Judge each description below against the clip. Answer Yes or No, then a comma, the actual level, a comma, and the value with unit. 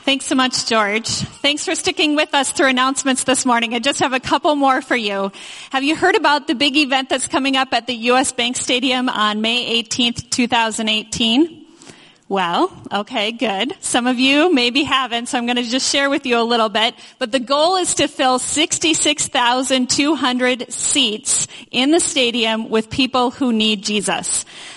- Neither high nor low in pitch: No, very high, 260 Hz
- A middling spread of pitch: Yes, average, 3.8 semitones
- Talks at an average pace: Yes, average, 180 wpm